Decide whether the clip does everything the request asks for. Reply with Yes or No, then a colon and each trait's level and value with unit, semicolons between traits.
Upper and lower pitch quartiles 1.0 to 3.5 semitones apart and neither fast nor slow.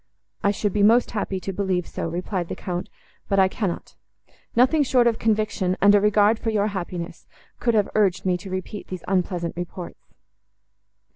Yes: average, 2.8 semitones; average, 175 wpm